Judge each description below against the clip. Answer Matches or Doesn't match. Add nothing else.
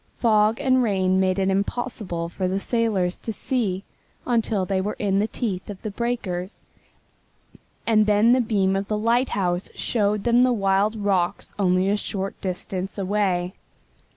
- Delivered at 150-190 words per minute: Matches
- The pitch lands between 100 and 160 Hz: Doesn't match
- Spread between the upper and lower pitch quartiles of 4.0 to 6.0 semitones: Doesn't match